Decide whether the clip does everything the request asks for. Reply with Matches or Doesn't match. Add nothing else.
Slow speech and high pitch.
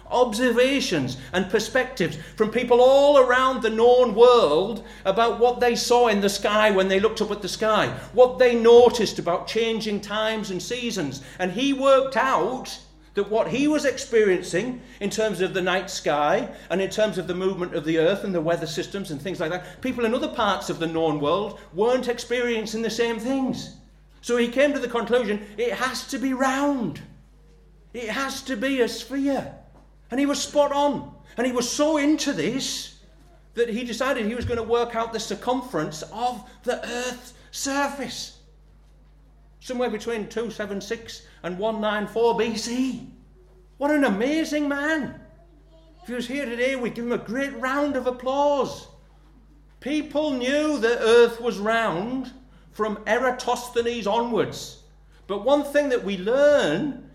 Doesn't match